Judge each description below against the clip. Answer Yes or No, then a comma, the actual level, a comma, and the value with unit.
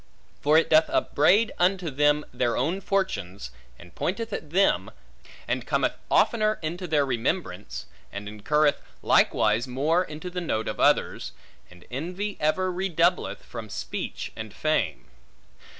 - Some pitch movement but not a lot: No, wide, 7.6 semitones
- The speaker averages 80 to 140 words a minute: Yes, slow, 135 wpm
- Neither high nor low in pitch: Yes, medium, 155 Hz